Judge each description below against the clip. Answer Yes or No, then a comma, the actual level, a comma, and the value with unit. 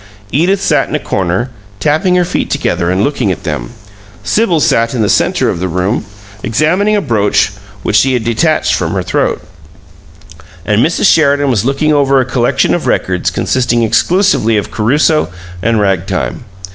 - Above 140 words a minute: Yes, average, 170 wpm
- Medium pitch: No, low, 120 Hz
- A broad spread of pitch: Yes, wide, 6.9 semitones